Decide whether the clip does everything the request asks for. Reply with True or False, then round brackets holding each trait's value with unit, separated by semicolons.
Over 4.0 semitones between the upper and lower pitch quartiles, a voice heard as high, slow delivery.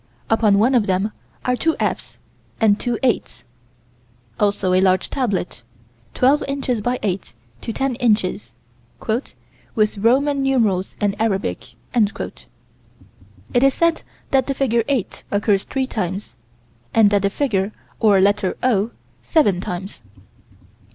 True (4.6 semitones; 215 Hz; 125 wpm)